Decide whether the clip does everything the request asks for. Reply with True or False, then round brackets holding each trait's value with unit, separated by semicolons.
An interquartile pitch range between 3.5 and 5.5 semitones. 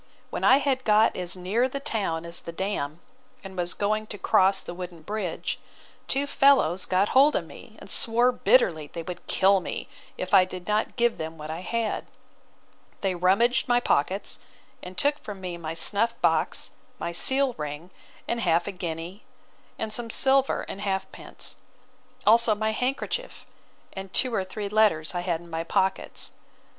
True (5.0 semitones)